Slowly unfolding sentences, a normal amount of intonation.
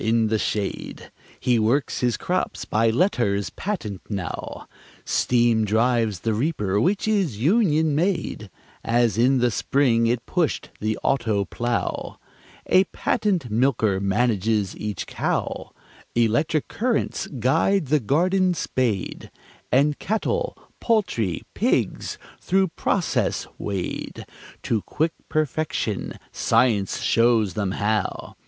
No: slow, 115 wpm; wide, 6.6 semitones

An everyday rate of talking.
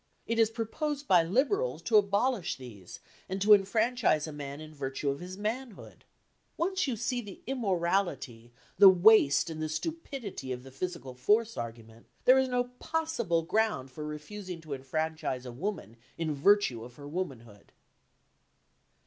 Yes: average, 155 wpm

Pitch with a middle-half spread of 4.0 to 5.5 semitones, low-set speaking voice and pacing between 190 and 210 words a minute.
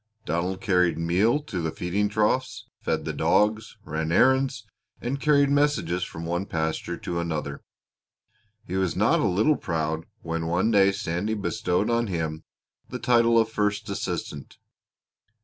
No: average, 5.2 semitones; very low, 95 Hz; average, 150 wpm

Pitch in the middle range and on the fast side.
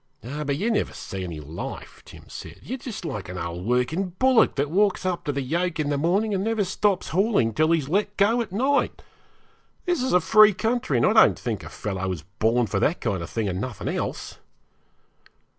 Yes: medium, 160 Hz; fast, 215 wpm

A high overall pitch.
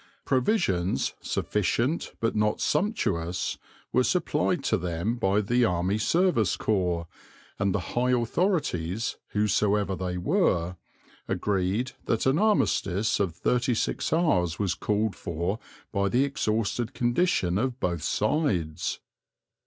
No: low, 105 Hz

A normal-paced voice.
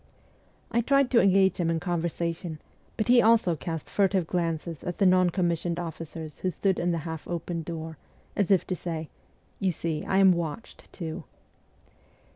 Yes: average, 175 wpm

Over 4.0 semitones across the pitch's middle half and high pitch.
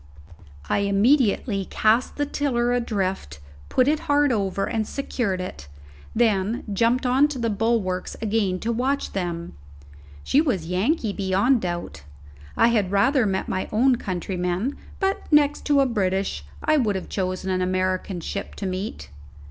Yes: average, 5.1 semitones; high, 210 Hz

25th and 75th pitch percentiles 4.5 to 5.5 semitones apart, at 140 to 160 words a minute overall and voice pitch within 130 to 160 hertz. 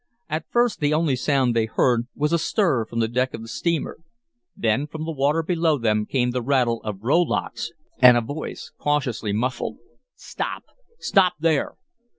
No: average, 5.2 semitones; average, 170 wpm; low, 135 Hz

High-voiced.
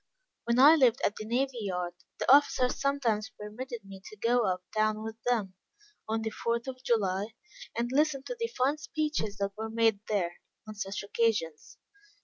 Yes: high, 225 Hz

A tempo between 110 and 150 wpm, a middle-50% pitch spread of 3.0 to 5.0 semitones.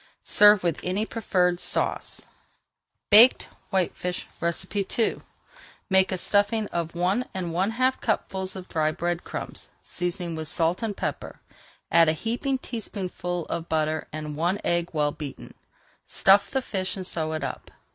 Yes: average, 145 wpm; average, 3.4 semitones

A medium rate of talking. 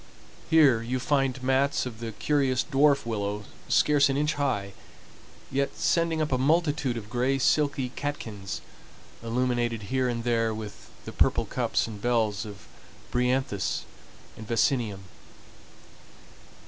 No: slow, 130 wpm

